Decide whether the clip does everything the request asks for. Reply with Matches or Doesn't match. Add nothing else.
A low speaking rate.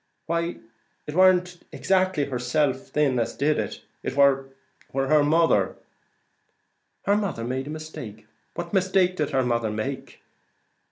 Matches